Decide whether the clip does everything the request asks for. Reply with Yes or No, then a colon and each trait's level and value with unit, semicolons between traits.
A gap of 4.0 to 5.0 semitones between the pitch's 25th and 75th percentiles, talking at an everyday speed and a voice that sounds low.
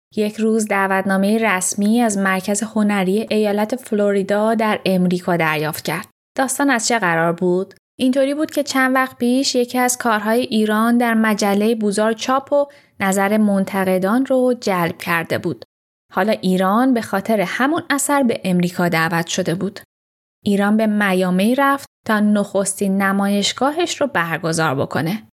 No: average, 4.3 semitones; average, 140 wpm; high, 210 Hz